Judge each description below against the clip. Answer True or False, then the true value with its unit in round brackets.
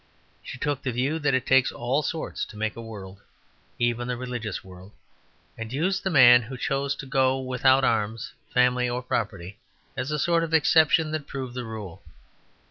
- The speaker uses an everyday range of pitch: True (3.5 semitones)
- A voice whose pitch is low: True (125 Hz)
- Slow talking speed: False (185 wpm)